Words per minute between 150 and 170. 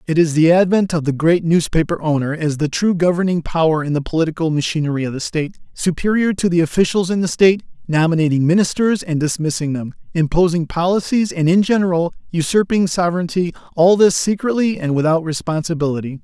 Yes: average, 165 wpm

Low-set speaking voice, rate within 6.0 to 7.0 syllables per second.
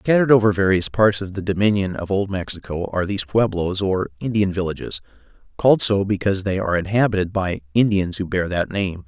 Yes: low, 100 Hz; 6.1 syllables/s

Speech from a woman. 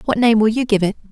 Yes: female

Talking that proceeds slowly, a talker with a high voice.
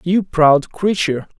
No: slow, 130 wpm; medium, 170 Hz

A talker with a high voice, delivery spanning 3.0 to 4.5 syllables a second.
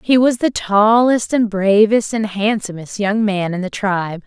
Yes: high, 210 Hz; 4.3 syllables/s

